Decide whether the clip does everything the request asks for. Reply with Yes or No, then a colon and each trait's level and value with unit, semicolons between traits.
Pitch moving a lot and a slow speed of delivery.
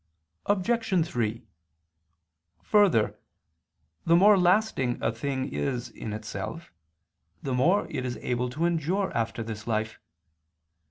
Yes: wide, 7.9 semitones; slow, 115 wpm